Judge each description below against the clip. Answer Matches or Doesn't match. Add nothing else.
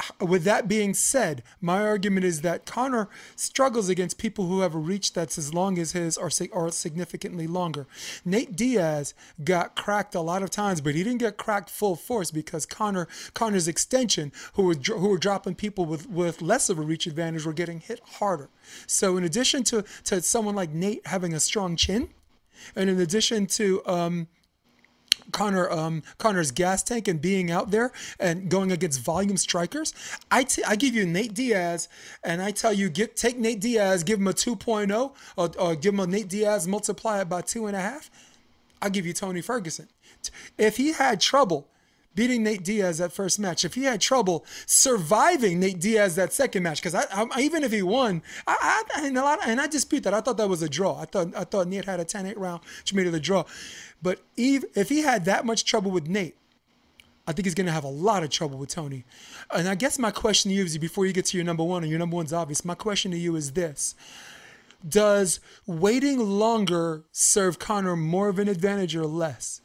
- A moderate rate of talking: Doesn't match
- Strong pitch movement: Doesn't match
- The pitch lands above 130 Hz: Matches